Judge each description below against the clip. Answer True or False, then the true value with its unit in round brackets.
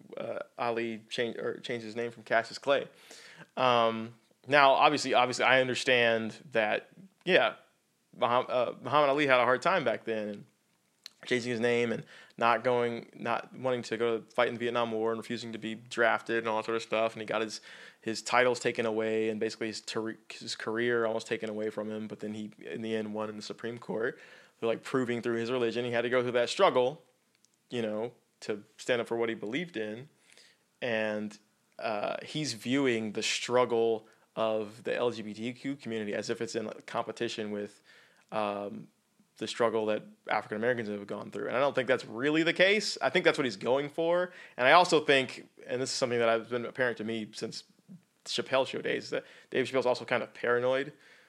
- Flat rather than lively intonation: True (2.3 semitones)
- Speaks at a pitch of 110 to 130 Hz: True (115 Hz)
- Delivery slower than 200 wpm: False (205 wpm)